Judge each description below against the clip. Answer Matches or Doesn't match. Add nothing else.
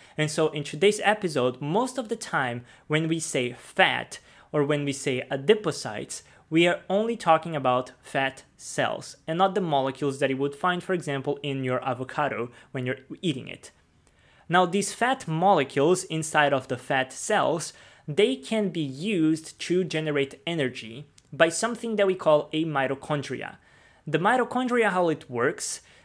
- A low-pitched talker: Doesn't match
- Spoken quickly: Doesn't match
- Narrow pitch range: Doesn't match